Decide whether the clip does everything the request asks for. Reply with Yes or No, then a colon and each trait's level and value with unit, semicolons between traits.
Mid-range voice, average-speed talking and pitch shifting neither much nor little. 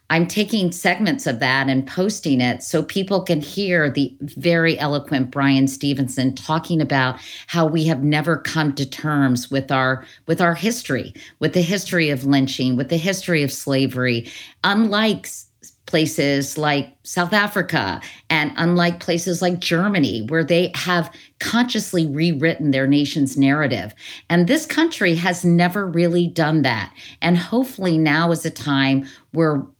Yes: medium, 160 Hz; average, 150 wpm; average, 4.2 semitones